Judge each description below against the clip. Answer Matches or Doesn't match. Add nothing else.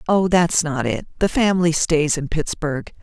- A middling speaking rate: Matches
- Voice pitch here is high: Doesn't match